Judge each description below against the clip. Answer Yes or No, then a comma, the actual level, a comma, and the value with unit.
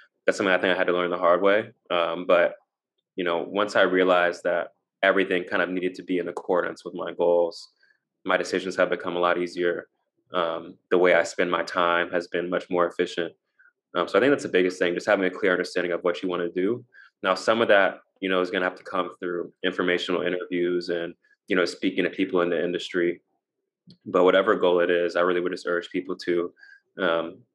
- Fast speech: Yes, fast, 230 wpm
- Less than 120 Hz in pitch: Yes, very low, 90 Hz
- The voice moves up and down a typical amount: No, narrow, 0.8 semitones